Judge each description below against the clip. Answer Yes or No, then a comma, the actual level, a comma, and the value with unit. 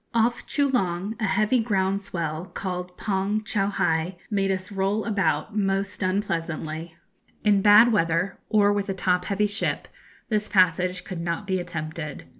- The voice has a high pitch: Yes, high, 195 Hz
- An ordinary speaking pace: Yes, average, 145 wpm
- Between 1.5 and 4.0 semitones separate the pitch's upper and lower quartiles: Yes, average, 2.7 semitones